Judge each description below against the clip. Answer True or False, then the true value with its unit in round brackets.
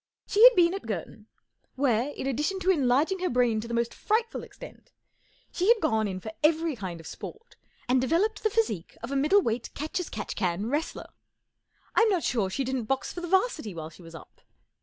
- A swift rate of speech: True (210 wpm)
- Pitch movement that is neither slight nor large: False (9.0 semitones)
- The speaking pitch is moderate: False (270 Hz)